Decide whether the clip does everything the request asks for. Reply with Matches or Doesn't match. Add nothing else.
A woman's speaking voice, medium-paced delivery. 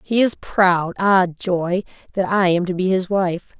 Matches